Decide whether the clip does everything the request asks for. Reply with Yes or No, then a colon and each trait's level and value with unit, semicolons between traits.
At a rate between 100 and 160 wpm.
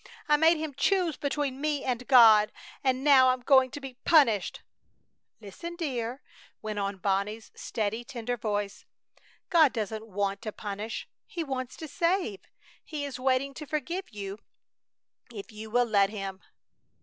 Yes: average, 150 wpm